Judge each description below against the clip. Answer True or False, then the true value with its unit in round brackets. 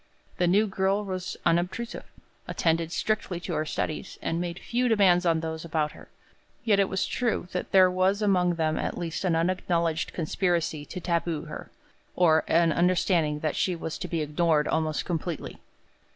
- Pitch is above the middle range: False (175 Hz)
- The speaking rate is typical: True (170 wpm)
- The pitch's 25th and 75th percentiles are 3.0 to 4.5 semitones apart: False (2.5 semitones)